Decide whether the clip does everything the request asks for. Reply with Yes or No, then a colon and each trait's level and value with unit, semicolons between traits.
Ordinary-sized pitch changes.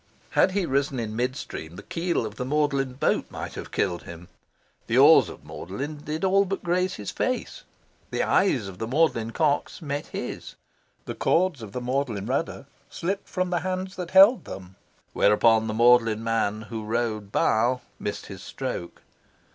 No: wide, 7.4 semitones